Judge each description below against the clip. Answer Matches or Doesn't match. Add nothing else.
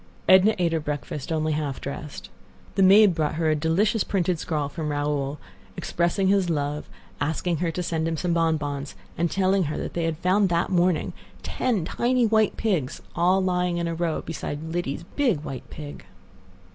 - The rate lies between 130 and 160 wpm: Doesn't match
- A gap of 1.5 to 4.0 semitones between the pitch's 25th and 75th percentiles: Matches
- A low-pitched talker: Doesn't match